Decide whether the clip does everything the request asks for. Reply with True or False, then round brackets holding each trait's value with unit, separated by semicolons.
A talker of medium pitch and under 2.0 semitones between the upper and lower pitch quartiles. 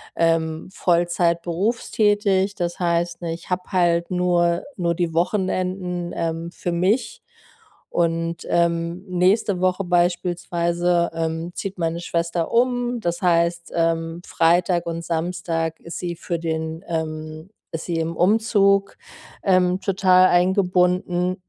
True (175 Hz; 1.6 semitones)